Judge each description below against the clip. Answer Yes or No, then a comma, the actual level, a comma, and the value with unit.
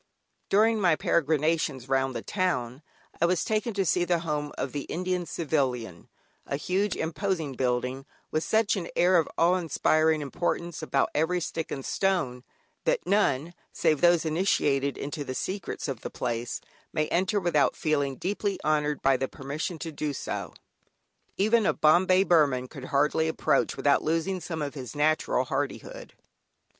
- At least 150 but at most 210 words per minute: Yes, average, 160 wpm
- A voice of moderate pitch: Yes, medium, 160 Hz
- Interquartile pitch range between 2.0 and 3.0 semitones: No, average, 4.5 semitones